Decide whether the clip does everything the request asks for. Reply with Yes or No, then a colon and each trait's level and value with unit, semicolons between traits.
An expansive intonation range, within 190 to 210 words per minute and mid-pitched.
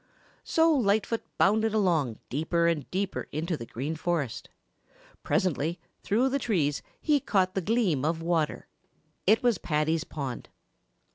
No: wide, 5.9 semitones; slow, 135 wpm; medium, 175 Hz